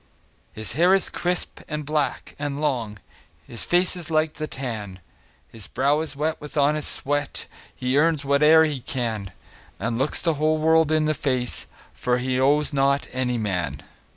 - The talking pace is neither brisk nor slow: Yes, average, 170 wpm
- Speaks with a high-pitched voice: No, medium, 145 Hz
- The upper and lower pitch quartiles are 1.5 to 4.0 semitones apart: Yes, average, 3.6 semitones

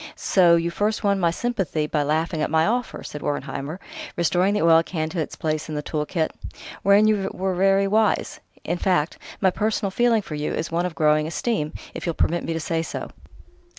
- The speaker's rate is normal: No, fast, 210 wpm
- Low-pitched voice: No, medium, 170 Hz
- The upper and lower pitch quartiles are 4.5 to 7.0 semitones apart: No, average, 4.0 semitones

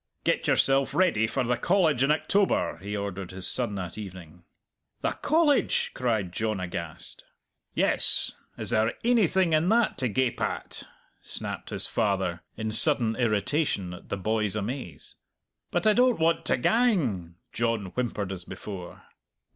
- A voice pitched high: No, low, 115 Hz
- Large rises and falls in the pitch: Yes, wide, 8.3 semitones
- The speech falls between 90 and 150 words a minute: Yes, average, 145 wpm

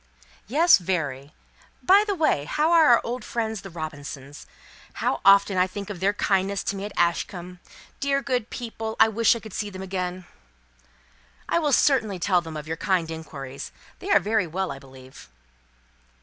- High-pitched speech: Yes, high, 195 Hz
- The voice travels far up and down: Yes, wide, 5.7 semitones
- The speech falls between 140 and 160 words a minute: No, average, 175 wpm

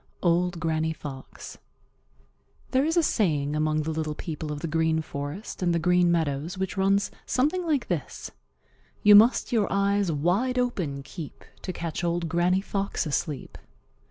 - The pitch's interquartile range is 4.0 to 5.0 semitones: Yes, average, 4.3 semitones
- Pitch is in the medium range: Yes, medium, 170 Hz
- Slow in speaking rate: No, average, 155 wpm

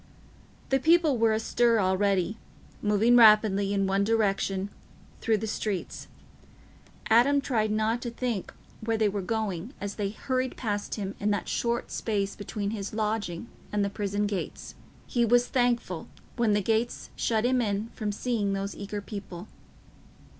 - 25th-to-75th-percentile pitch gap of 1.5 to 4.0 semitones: Yes, narrow, 2.5 semitones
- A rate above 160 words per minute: No, average, 155 wpm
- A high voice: Yes, high, 215 Hz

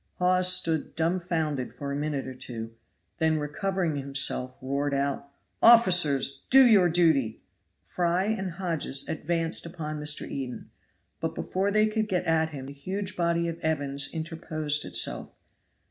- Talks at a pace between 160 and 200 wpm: No, average, 145 wpm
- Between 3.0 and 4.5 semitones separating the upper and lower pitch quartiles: Yes, average, 4.2 semitones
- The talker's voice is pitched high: No, medium, 160 Hz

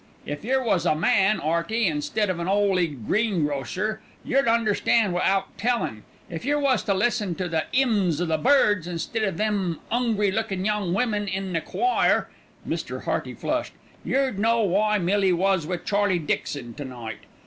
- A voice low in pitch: No, high, 195 Hz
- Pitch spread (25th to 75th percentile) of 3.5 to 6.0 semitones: Yes, average, 4.4 semitones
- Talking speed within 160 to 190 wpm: Yes, average, 170 wpm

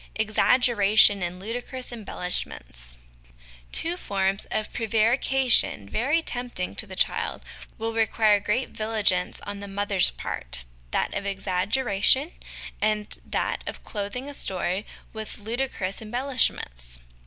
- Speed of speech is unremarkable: No, slow, 115 wpm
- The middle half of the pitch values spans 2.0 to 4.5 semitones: Yes, average, 3.9 semitones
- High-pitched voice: Yes, high, 210 Hz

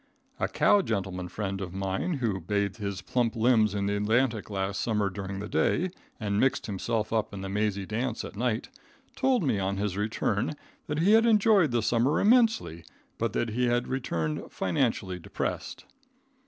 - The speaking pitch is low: Yes, low, 105 Hz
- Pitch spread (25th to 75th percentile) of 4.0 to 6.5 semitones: Yes, average, 4.3 semitones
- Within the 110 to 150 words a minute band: No, average, 175 wpm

